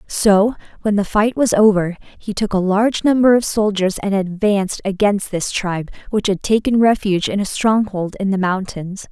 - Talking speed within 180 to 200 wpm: Yes, average, 185 wpm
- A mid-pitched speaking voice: No, high, 200 Hz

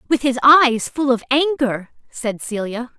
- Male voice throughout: No, female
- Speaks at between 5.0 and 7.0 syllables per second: No, 4.0 syllables/s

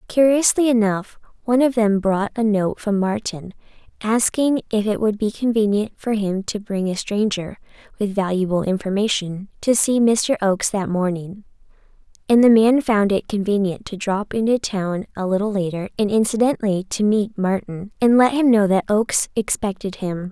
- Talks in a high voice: Yes, high, 210 Hz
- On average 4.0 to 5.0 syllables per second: Yes, 4.9 syllables/s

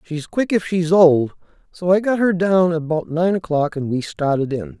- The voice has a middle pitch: Yes, medium, 165 Hz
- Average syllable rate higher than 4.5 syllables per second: Yes, 4.9 syllables/s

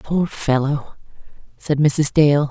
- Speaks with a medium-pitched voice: Yes, medium, 145 Hz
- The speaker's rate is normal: No, slow, 120 wpm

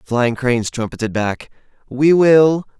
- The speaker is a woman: No, male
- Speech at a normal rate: Yes, average, 150 wpm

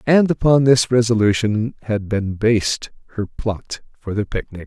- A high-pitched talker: No, low, 110 Hz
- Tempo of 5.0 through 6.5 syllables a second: No, 4.4 syllables/s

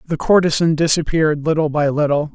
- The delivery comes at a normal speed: Yes, average, 155 wpm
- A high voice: No, medium, 155 Hz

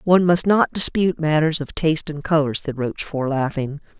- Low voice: No, medium, 155 Hz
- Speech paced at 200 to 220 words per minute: No, average, 180 wpm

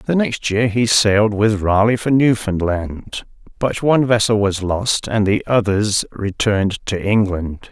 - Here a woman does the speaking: No, male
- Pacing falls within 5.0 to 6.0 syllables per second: No, 4.1 syllables/s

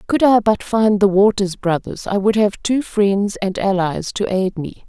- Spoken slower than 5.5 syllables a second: Yes, 4.3 syllables/s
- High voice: Yes, high, 200 Hz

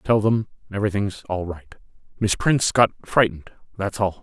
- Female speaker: No, male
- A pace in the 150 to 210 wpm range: No, average, 140 wpm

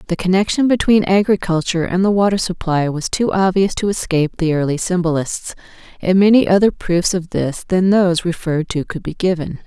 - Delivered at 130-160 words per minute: No, average, 180 wpm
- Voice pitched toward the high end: No, medium, 180 Hz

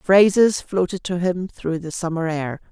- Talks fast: No, average, 175 wpm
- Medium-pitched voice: Yes, medium, 175 Hz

